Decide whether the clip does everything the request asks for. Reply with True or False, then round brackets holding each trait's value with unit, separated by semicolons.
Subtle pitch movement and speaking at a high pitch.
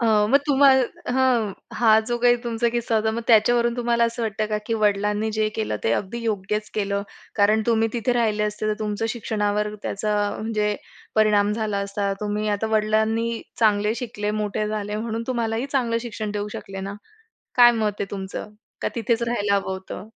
True (2.0 semitones; 215 Hz)